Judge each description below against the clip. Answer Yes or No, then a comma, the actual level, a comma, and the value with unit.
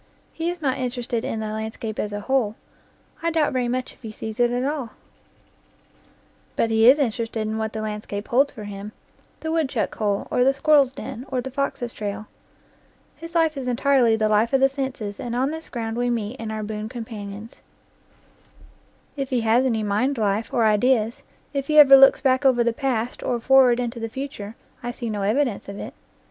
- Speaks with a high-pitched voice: Yes, high, 240 Hz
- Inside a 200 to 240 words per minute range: Yes, fast, 205 wpm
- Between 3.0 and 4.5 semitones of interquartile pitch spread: Yes, average, 3.6 semitones